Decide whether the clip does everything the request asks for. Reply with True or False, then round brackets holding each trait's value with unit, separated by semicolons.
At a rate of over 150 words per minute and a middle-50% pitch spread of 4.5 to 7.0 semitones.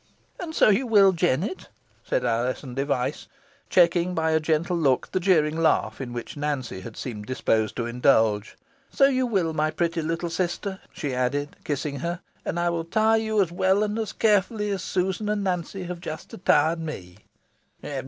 True (175 wpm; 5.3 semitones)